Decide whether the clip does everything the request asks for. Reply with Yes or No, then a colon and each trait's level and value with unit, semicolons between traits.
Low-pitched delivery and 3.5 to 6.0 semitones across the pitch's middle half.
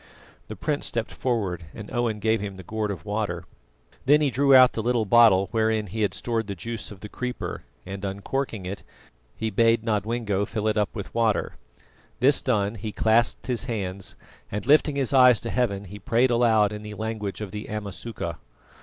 No: low, 110 Hz; average, 2.8 semitones